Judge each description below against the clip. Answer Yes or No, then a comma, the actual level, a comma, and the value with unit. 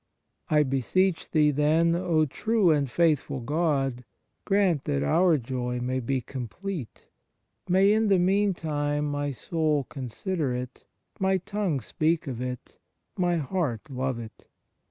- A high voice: No, medium, 150 Hz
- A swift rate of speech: No, slow, 135 wpm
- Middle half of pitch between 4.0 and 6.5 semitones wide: Yes, average, 5.2 semitones